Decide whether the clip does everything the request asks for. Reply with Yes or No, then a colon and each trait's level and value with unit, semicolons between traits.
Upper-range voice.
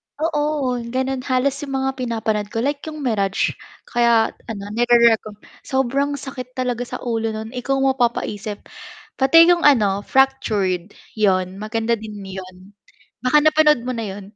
Yes: high, 240 Hz